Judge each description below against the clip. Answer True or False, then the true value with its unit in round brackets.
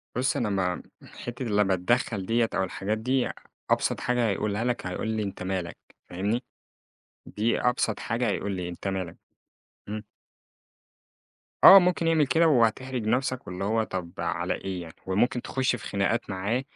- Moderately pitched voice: False (110 Hz)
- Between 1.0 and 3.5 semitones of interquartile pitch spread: False (4.3 semitones)